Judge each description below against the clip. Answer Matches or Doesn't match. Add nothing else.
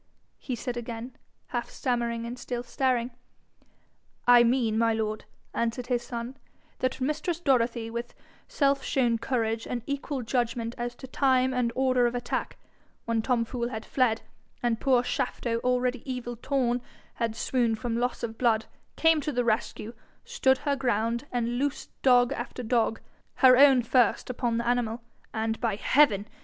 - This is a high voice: Matches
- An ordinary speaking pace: Matches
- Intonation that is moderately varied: Doesn't match